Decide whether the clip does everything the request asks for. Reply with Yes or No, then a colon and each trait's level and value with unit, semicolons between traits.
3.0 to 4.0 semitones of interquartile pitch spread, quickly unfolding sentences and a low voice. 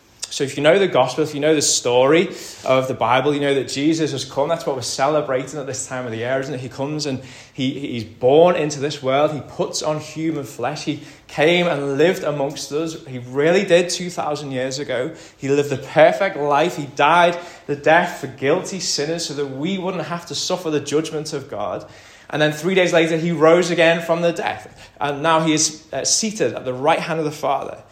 No: average, 3.3 semitones; fast, 225 wpm; medium, 150 Hz